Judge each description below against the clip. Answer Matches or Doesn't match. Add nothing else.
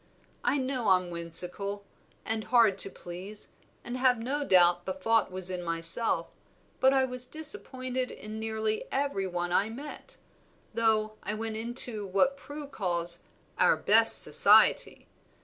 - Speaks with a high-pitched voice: Matches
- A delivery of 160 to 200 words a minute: Doesn't match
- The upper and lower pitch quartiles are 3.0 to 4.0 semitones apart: Doesn't match